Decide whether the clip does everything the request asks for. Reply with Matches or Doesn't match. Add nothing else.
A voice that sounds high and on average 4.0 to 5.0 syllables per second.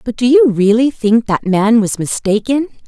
Matches